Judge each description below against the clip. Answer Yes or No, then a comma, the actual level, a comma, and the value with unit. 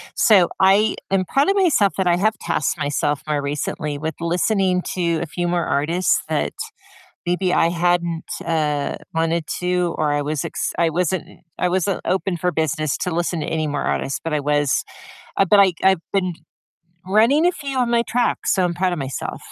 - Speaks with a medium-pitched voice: Yes, medium, 175 Hz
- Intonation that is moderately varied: Yes, average, 3.4 semitones